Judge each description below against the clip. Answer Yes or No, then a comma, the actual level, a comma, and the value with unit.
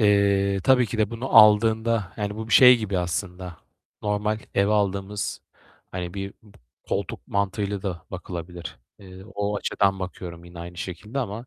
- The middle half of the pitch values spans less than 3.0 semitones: Yes, narrow, 2.5 semitones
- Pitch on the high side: No, low, 100 Hz